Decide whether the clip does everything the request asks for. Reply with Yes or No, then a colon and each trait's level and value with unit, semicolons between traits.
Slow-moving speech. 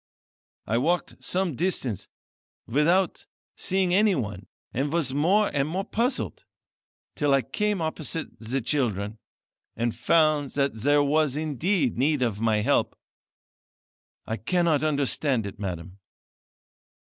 Yes: slow, 120 wpm